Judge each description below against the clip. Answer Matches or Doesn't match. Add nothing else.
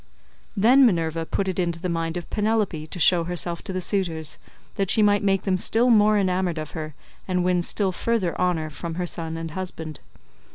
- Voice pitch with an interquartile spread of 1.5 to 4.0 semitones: Matches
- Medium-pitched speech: Matches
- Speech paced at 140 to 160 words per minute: Doesn't match